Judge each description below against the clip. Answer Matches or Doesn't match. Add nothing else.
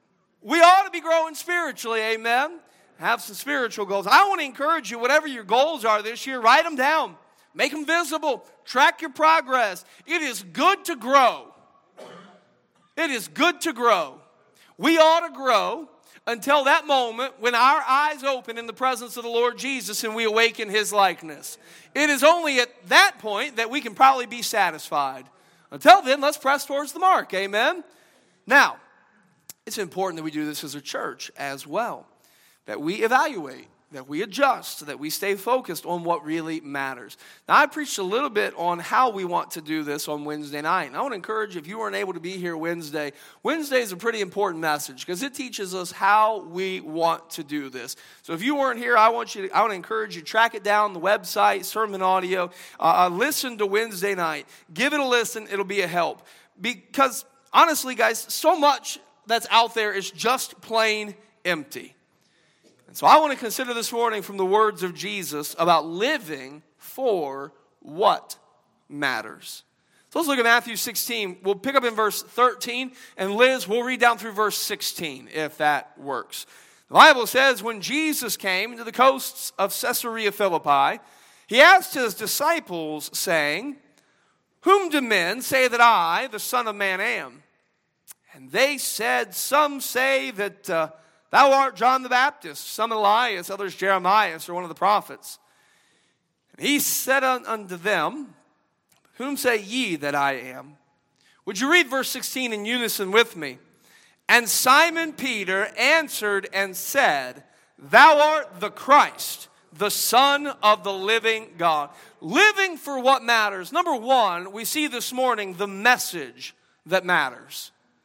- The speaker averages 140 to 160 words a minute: Doesn't match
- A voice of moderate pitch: Doesn't match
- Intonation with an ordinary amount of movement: Doesn't match